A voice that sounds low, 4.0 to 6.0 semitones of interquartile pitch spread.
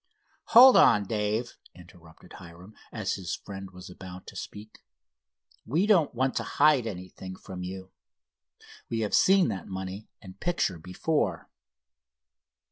Yes: low, 100 Hz; average, 4.6 semitones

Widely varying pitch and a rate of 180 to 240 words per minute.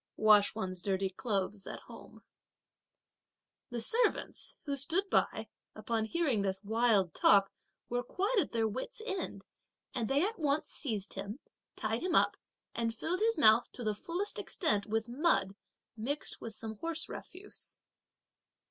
No: wide, 7.9 semitones; average, 150 wpm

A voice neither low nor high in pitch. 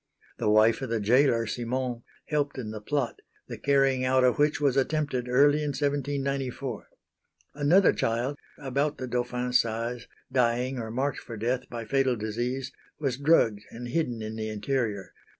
No: low, 125 Hz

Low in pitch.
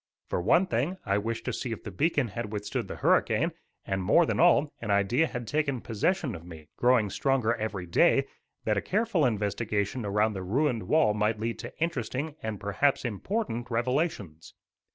Yes: low, 115 Hz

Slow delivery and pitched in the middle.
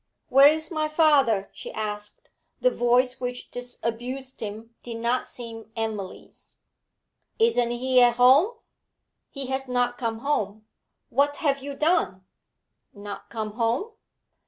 No: slow, 130 wpm; high, 245 Hz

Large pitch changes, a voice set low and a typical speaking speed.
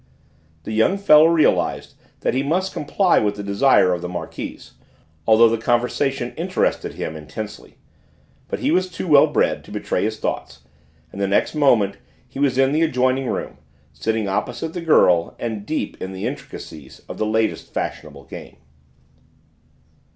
Yes: wide, 6.8 semitones; low, 120 Hz; average, 160 wpm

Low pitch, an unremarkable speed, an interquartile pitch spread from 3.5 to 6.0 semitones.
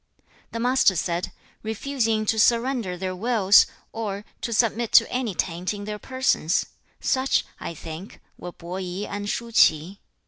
No: high, 210 Hz; average, 160 wpm; average, 4.2 semitones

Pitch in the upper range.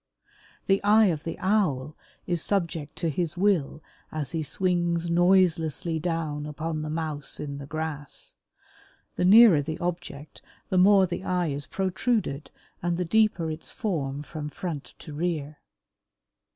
No: medium, 165 Hz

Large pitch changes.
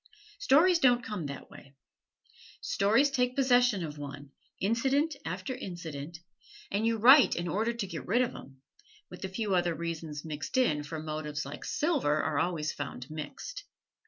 Yes: wide, 8.4 semitones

